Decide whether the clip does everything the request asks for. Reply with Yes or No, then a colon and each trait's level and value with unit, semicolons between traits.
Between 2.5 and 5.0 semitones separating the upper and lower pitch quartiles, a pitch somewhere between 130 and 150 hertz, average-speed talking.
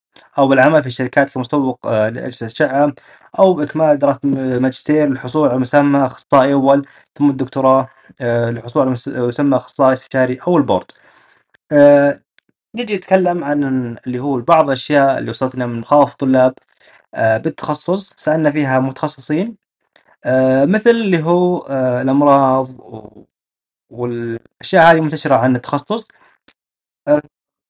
Yes: average, 2.9 semitones; medium, 140 Hz; average, 115 wpm